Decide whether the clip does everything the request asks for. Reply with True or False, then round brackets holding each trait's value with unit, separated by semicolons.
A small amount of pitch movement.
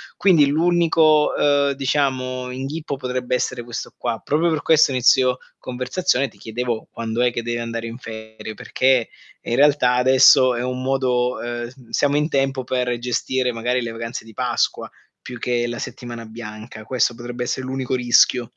True (2.1 semitones)